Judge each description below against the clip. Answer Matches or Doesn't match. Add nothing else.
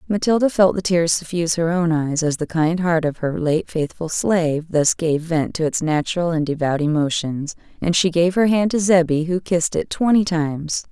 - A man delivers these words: Doesn't match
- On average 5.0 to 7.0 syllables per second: Matches